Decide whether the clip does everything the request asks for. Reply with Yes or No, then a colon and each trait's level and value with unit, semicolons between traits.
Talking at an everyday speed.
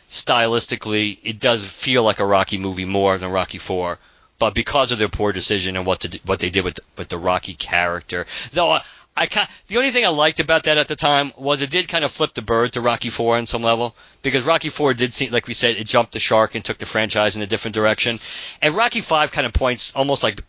No: fast, 250 wpm